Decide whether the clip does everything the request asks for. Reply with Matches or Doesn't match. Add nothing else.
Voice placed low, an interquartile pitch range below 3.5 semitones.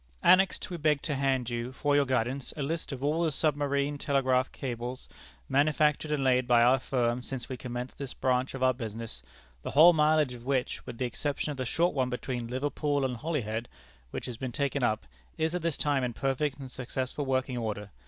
Matches